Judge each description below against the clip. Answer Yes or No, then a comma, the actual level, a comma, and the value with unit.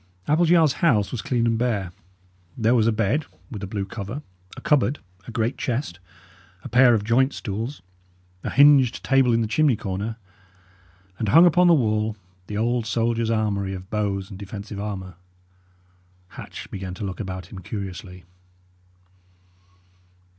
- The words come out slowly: No, average, 155 wpm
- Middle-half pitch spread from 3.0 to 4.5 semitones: Yes, average, 4.1 semitones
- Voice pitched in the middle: No, low, 110 Hz